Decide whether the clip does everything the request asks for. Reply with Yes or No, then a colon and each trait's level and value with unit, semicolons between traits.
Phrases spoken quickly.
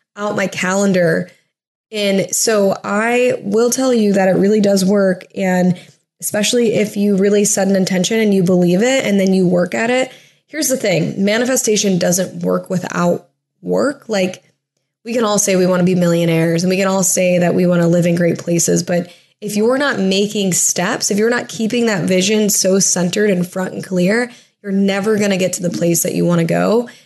Yes: fast, 210 wpm